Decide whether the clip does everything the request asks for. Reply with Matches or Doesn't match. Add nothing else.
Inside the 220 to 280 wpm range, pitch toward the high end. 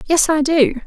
Doesn't match